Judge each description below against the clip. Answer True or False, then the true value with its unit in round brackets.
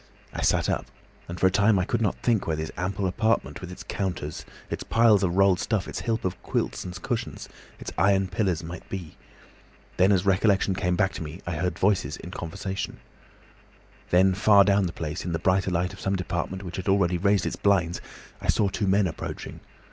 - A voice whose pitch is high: False (95 Hz)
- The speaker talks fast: True (210 wpm)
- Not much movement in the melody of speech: True (2.0 semitones)